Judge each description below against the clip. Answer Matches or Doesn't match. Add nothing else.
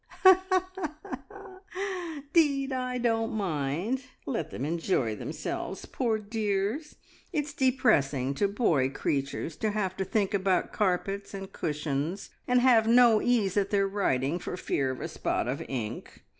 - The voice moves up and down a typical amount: Doesn't match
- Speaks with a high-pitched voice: Matches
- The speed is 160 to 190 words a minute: Doesn't match